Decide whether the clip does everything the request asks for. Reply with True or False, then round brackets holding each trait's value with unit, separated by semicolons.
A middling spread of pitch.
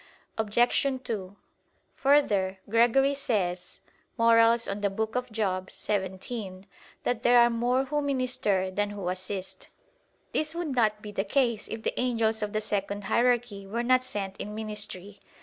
True (3.5 semitones)